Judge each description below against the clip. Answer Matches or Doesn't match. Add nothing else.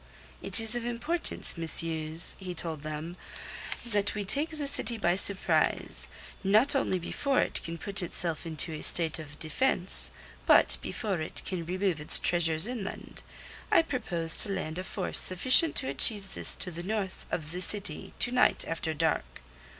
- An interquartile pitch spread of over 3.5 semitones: Matches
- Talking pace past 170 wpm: Doesn't match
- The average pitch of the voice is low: Doesn't match